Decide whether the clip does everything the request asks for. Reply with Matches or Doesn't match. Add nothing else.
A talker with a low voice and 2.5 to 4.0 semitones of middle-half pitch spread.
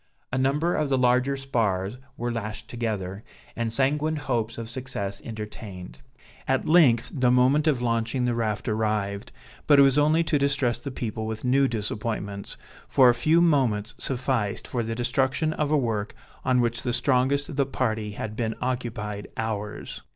Matches